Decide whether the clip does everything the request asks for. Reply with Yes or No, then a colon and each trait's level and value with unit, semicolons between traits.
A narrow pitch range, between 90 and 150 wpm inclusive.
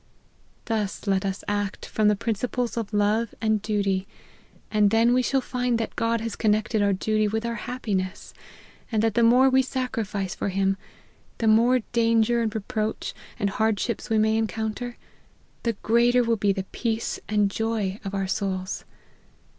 No: narrow, 2.2 semitones; average, 170 wpm